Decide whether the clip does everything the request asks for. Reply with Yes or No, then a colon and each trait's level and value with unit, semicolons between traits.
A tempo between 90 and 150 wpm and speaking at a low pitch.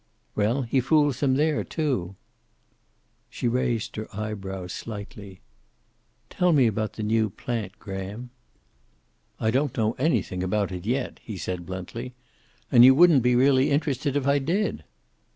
Yes: average, 145 wpm; low, 120 Hz